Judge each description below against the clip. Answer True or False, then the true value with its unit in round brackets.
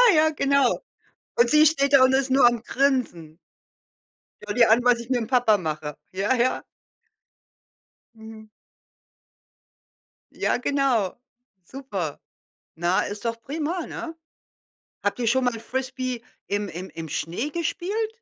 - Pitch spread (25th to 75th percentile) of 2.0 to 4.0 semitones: False (4.8 semitones)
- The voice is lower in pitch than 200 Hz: False (245 Hz)